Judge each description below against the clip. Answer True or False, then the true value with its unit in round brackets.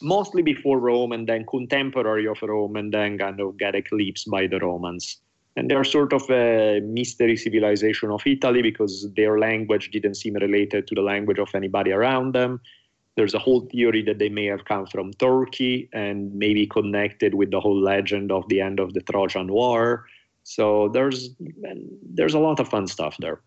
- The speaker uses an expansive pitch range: False (3.7 semitones)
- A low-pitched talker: True (110 Hz)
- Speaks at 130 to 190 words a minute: True (185 wpm)